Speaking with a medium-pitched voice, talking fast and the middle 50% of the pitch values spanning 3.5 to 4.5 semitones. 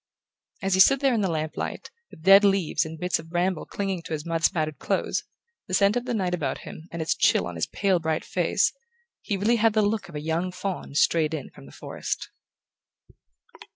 Yes: medium, 180 Hz; fast, 220 wpm; average, 3.8 semitones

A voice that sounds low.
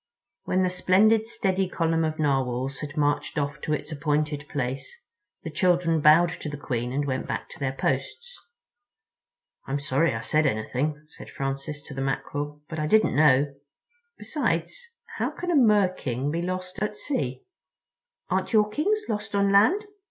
No: medium, 155 Hz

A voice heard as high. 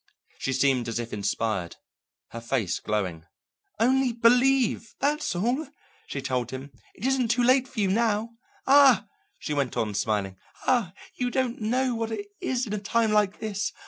Yes: high, 210 Hz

